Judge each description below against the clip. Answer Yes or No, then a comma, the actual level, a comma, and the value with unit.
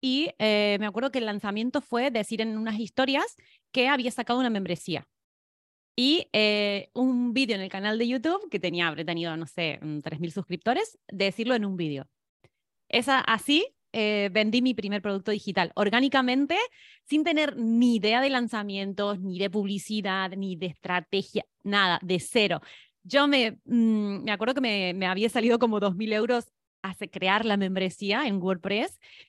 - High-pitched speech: Yes, high, 215 Hz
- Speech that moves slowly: No, average, 165 wpm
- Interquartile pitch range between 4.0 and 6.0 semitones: Yes, average, 4.4 semitones